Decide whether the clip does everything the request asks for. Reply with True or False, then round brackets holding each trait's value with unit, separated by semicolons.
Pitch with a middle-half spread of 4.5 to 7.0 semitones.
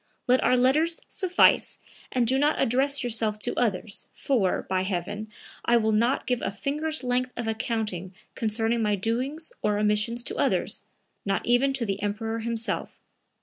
False (3.3 semitones)